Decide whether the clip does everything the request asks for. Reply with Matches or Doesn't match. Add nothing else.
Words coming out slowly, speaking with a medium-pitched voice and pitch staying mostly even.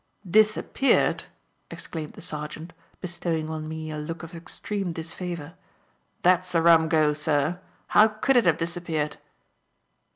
Matches